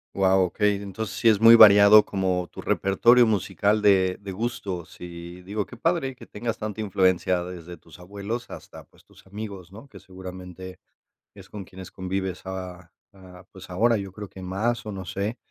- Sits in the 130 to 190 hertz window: No, very low, 95 Hz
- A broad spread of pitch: No, narrow, 2.6 semitones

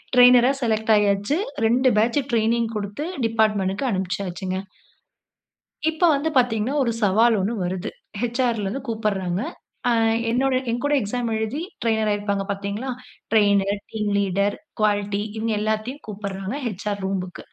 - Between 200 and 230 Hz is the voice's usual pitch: Yes, high, 215 Hz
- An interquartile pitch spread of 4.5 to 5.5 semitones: No, average, 2.9 semitones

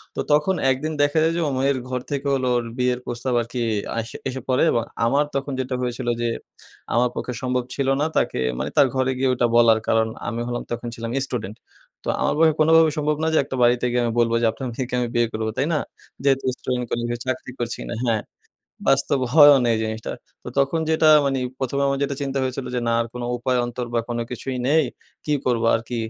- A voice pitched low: Yes, low, 125 Hz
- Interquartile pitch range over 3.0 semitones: No, average, 2.7 semitones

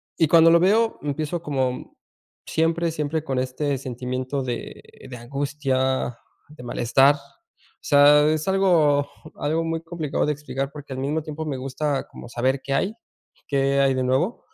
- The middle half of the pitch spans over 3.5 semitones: No, average, 3.1 semitones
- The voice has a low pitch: No, medium, 145 Hz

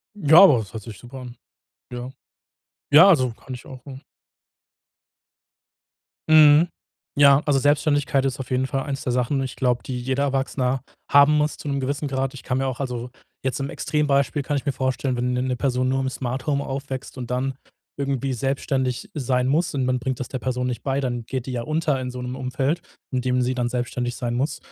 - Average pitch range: No, narrow, 1.8 semitones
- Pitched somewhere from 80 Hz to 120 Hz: No, low, 130 Hz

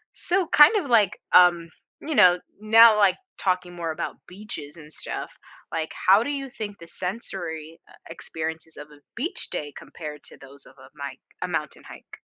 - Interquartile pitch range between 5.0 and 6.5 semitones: Yes, average, 5.3 semitones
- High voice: No, medium, 180 Hz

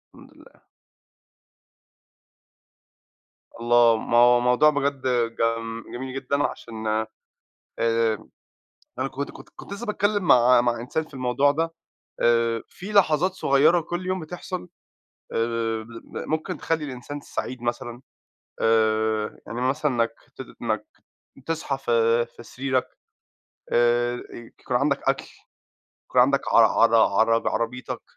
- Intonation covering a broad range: No, average, 3.9 semitones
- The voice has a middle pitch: No, low, 125 Hz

